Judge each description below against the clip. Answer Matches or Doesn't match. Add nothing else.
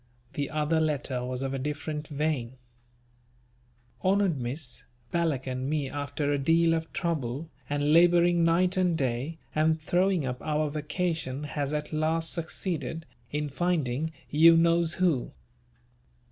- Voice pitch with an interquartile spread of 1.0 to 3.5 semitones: Matches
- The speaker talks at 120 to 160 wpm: Matches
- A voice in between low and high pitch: Matches